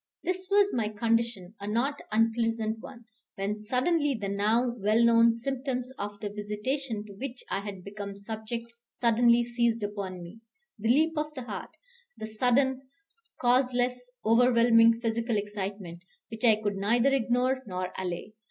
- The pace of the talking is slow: No, average, 150 wpm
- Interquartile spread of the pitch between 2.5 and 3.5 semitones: Yes, average, 3.1 semitones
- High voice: Yes, high, 230 Hz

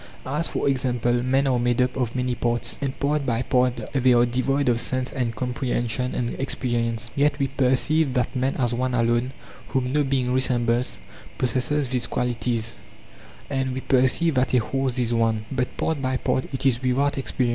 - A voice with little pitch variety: Yes, narrow, 1.8 semitones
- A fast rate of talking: No, average, 185 wpm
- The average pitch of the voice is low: Yes, low, 125 Hz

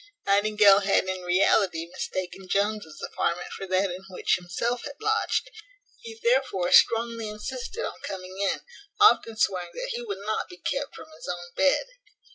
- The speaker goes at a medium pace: Yes, average, 160 wpm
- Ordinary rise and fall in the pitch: No, wide, 6.9 semitones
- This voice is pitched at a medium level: No, high, 200 Hz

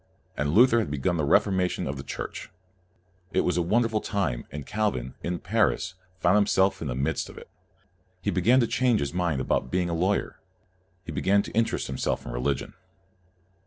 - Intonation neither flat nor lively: No, wide, 6.5 semitones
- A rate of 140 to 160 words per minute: No, average, 190 wpm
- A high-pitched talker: No, very low, 90 Hz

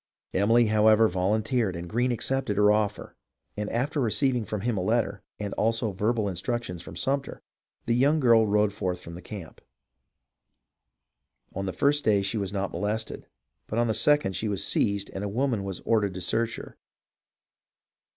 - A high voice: No, low, 105 Hz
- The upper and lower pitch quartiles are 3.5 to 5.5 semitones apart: No, average, 3.1 semitones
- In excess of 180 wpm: No, average, 175 wpm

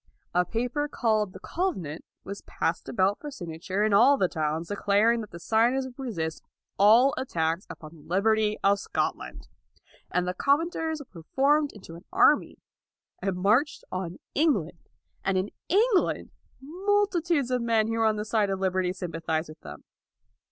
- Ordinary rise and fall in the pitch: No, wide, 6.9 semitones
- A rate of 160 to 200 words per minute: Yes, average, 165 wpm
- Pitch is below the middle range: No, high, 210 Hz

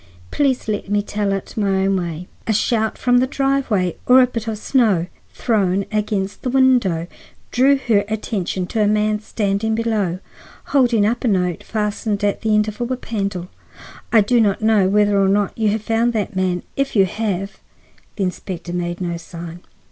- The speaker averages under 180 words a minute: No, average, 185 wpm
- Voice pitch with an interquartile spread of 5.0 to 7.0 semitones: No, average, 3.0 semitones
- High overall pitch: Yes, high, 210 Hz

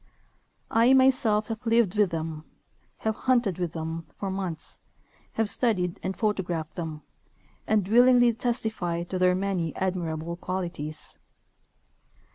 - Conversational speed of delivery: No, slow, 120 wpm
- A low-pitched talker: No, high, 190 Hz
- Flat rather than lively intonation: No, average, 4.8 semitones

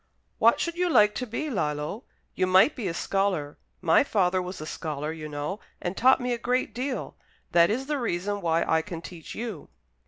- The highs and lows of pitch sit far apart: Yes, wide, 6.7 semitones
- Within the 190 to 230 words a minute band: Yes, average, 200 wpm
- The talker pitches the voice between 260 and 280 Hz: No, high, 190 Hz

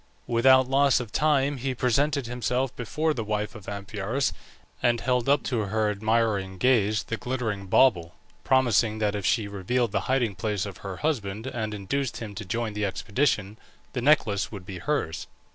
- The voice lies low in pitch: Yes, low, 115 Hz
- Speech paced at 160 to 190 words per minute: Yes, average, 175 wpm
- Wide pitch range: No, average, 4.2 semitones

